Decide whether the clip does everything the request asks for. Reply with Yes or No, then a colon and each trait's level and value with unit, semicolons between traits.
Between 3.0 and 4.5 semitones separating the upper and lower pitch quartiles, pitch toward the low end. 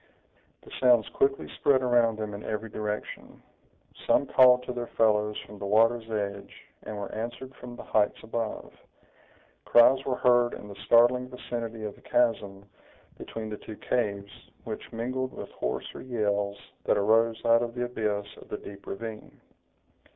No: narrow, 2.6 semitones; low, 115 Hz